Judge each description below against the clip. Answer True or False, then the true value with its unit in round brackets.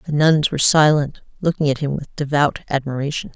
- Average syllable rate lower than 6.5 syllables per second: True (5.8 syllables/s)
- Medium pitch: True (145 Hz)